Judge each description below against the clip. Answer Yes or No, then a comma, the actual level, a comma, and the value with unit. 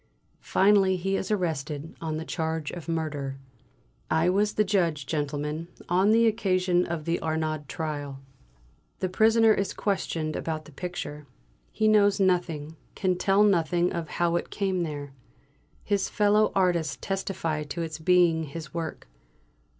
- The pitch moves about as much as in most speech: Yes, average, 3.7 semitones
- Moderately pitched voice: Yes, medium, 170 Hz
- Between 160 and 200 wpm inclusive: No, average, 145 wpm